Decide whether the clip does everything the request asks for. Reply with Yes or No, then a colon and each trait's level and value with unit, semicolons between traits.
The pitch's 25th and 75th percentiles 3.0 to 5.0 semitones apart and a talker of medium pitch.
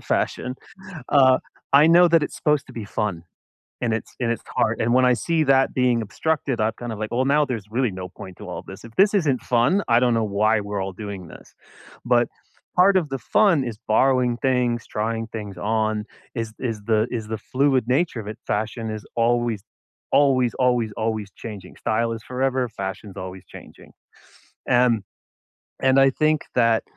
No: average, 3.4 semitones; low, 120 Hz